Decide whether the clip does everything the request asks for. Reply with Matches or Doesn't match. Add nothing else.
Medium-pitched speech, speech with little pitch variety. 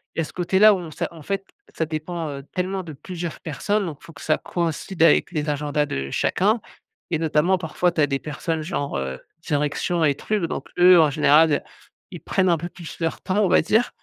Doesn't match